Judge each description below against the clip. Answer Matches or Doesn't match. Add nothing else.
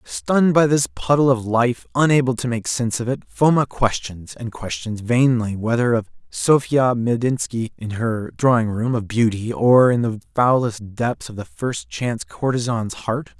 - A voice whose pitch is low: Matches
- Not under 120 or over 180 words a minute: Matches